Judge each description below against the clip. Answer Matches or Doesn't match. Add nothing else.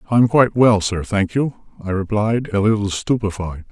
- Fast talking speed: Doesn't match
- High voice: Doesn't match